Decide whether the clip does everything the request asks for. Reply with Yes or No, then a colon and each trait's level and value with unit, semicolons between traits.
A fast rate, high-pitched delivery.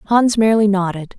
No: average, 150 wpm; high, 205 Hz